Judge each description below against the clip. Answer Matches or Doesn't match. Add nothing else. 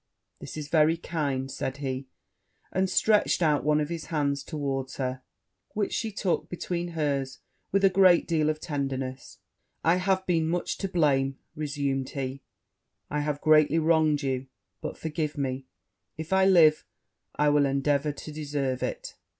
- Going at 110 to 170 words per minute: Matches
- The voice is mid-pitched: Matches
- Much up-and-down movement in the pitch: Doesn't match